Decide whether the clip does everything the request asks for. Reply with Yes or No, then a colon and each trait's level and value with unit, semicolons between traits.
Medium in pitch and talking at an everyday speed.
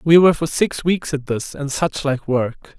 No: medium, 150 Hz; fast, 235 wpm